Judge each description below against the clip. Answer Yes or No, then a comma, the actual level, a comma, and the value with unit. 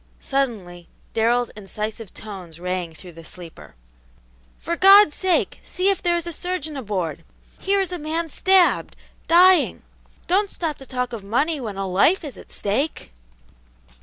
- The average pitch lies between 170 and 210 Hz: No, very high, 260 Hz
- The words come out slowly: No, average, 155 wpm